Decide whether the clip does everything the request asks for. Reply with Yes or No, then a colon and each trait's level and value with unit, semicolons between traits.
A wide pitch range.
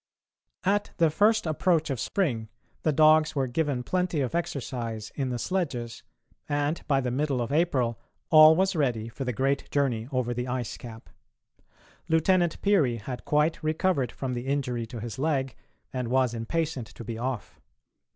No: average, 4.6 semitones